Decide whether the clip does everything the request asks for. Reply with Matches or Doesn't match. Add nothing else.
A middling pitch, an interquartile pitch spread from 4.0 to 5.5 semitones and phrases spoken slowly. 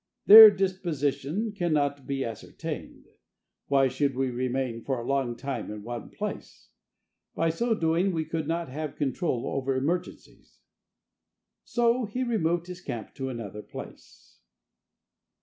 Matches